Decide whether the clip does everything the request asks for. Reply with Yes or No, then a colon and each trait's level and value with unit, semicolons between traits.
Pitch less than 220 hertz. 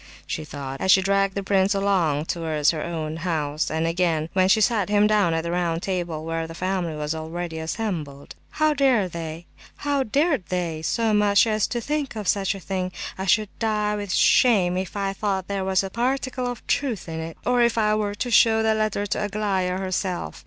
Yes: high, 190 Hz